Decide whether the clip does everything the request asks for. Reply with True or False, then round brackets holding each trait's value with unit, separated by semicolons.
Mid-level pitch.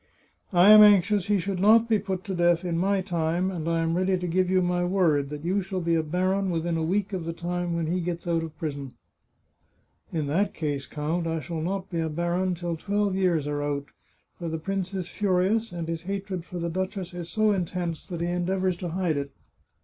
True (175 Hz)